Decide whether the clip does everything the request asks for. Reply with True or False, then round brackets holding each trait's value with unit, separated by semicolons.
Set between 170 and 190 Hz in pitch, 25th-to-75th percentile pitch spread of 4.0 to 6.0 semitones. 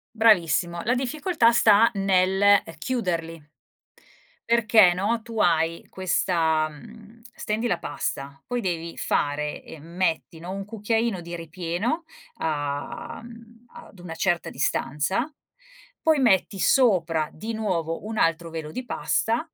True (185 Hz; 5.5 semitones)